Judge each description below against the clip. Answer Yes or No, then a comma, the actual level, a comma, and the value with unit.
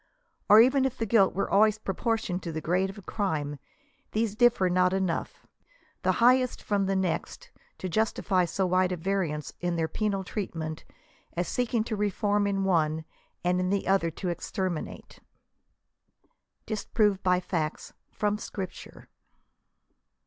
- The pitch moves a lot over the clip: No, average, 3.1 semitones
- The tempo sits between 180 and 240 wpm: No, average, 150 wpm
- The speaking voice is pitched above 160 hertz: Yes, high, 190 Hz